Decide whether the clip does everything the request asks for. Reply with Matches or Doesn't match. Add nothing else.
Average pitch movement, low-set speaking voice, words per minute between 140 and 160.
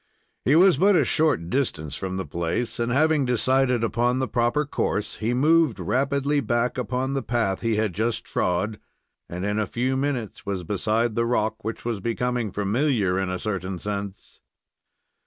Doesn't match